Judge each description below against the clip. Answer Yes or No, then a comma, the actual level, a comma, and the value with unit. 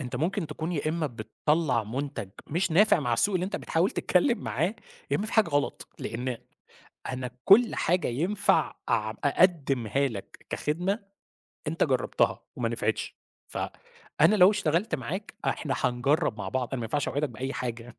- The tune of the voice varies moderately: No, wide, 6.7 semitones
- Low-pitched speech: No, medium, 150 Hz